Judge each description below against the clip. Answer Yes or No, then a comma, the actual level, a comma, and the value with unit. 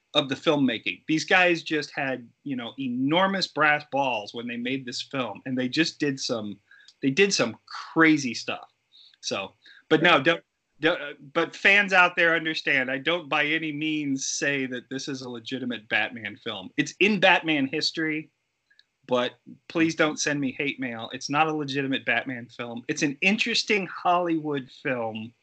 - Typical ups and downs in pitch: Yes, average, 3.9 semitones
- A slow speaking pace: No, average, 170 wpm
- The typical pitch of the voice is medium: Yes, medium, 150 Hz